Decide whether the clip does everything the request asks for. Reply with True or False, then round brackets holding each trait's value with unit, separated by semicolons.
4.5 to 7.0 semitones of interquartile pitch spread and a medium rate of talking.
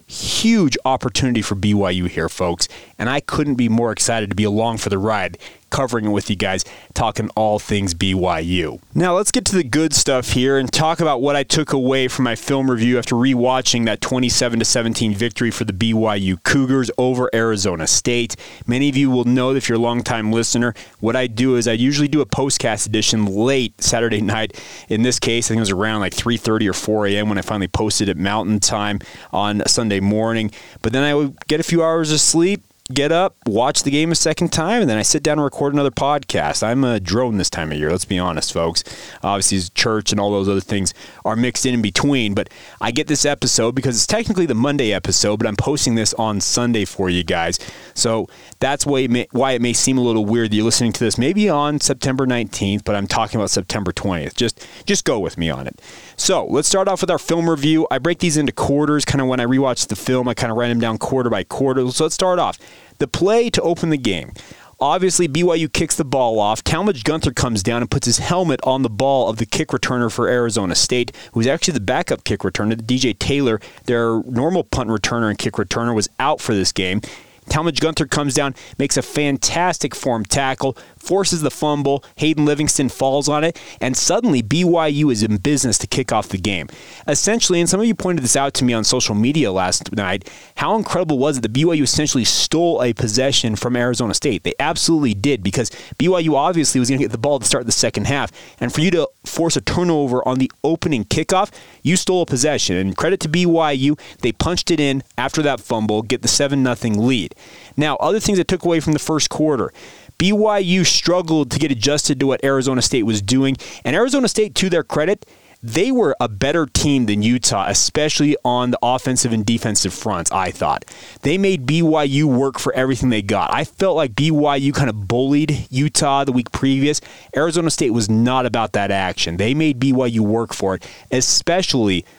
False (5.1 semitones; 215 wpm)